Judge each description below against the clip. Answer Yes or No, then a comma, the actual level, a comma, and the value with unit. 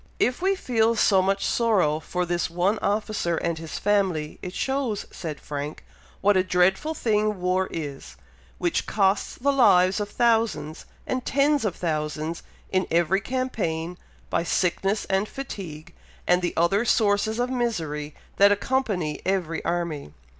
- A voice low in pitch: No, high, 190 Hz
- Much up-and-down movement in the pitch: No, average, 4.8 semitones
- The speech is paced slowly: No, average, 145 wpm